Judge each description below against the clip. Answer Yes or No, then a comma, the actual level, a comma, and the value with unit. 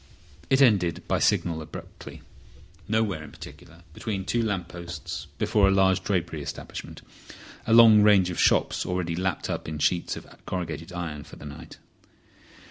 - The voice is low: Yes, very low, 90 Hz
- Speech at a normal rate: Yes, average, 150 wpm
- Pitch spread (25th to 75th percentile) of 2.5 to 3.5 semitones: Yes, average, 3.2 semitones